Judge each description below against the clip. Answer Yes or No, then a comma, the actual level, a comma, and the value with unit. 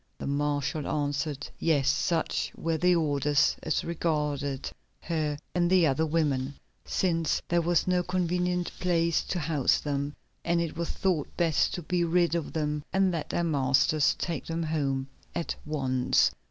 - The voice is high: No, medium, 160 Hz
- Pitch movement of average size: Yes, average, 3.0 semitones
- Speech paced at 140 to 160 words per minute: Yes, average, 155 wpm